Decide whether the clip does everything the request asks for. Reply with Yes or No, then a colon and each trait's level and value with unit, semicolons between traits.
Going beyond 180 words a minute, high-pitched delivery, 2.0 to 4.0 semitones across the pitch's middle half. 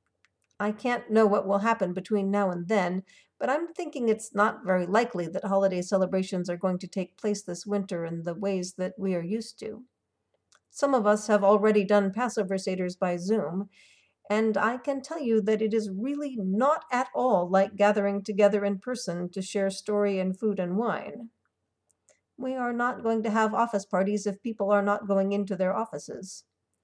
Yes: average, 190 wpm; high, 205 Hz; average, 2.8 semitones